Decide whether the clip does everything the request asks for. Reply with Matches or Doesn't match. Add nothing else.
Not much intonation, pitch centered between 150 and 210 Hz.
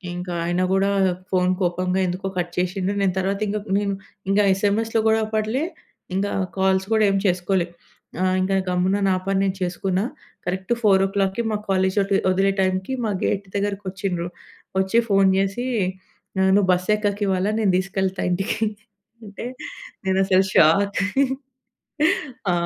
Matches